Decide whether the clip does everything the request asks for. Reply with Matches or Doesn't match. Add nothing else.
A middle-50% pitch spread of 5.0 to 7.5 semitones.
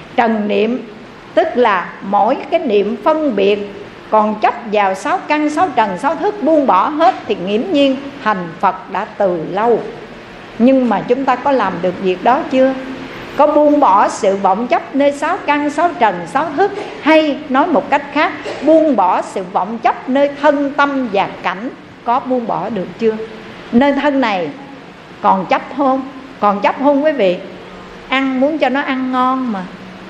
Matches